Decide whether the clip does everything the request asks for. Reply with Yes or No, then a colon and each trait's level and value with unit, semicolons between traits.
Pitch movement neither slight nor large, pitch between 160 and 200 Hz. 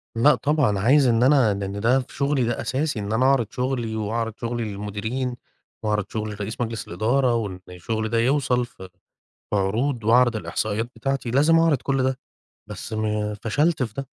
No: average, 3.7 semitones; low, 115 Hz